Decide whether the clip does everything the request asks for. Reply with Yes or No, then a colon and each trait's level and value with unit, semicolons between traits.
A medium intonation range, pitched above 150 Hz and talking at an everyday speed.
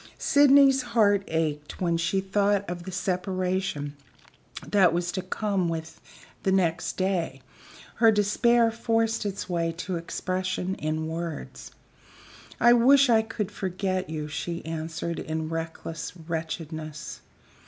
No: average, 3.9 semitones; medium, 185 Hz; slow, 125 wpm